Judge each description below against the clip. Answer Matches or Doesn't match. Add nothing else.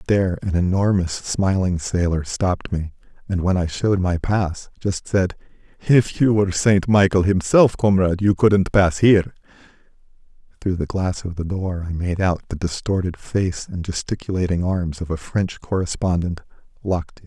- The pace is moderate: Matches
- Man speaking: Matches